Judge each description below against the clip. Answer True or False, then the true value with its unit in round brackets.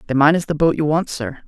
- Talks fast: True (325 wpm)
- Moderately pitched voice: True (150 Hz)